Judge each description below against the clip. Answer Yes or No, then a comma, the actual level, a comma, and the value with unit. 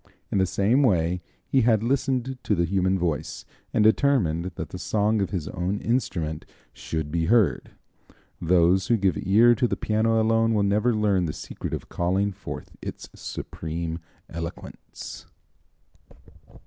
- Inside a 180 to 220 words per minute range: No, average, 150 wpm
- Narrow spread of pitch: No, average, 4.6 semitones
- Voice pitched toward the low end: Yes, low, 100 Hz